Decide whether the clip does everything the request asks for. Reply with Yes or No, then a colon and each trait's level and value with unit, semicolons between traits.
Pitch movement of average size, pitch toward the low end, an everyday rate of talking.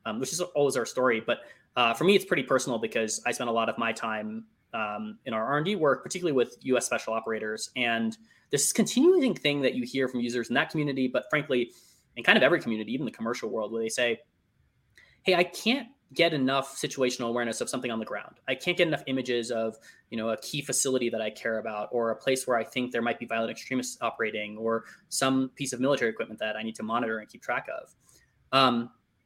No: average, 3.6 semitones; low, 125 Hz; fast, 235 wpm